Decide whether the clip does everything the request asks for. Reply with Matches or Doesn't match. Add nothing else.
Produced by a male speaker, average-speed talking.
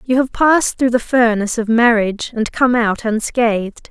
Doesn't match